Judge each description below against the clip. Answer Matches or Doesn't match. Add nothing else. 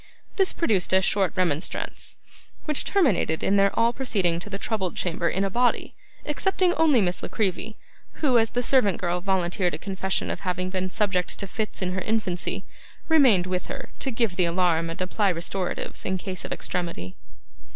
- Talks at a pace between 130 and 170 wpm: Doesn't match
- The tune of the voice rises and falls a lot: Doesn't match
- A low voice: Doesn't match